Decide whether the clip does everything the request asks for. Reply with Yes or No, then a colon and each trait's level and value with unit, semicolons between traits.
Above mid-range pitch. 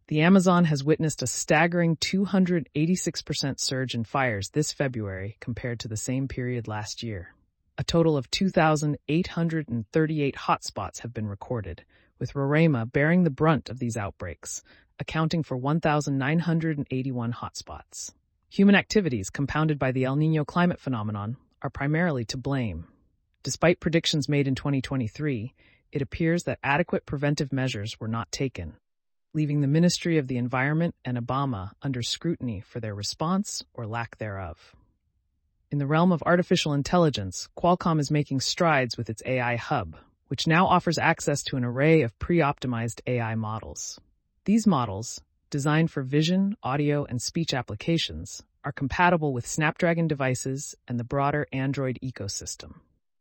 No: medium, 140 Hz